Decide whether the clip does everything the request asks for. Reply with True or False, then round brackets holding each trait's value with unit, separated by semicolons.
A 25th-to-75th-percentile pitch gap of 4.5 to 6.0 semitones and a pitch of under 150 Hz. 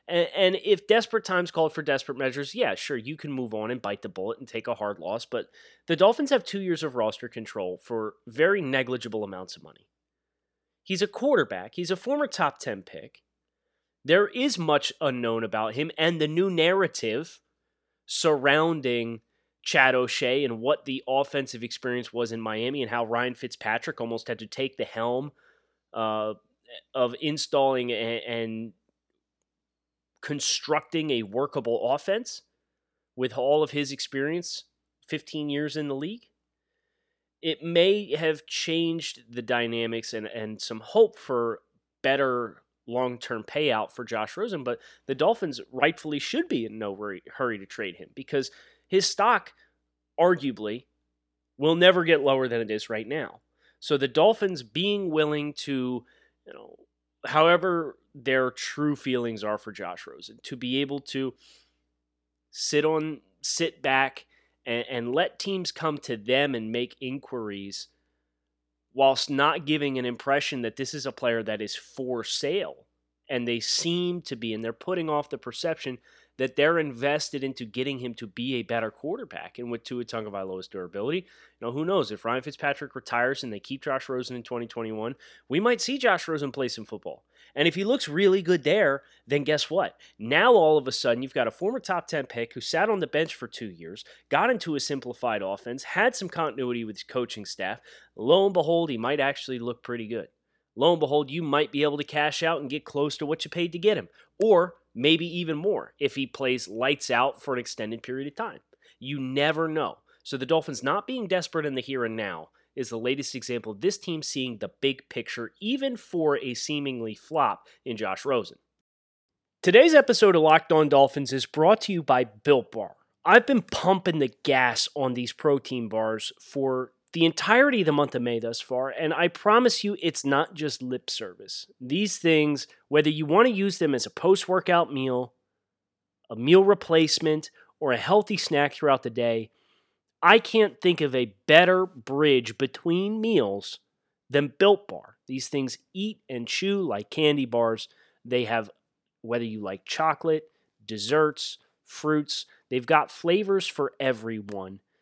True (5.3 semitones; 140 Hz)